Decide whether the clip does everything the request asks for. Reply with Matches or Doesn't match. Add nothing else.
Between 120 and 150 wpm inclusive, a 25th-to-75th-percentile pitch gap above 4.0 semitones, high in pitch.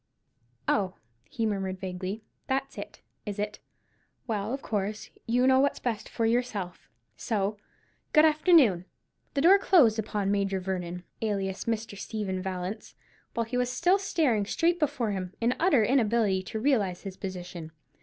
Matches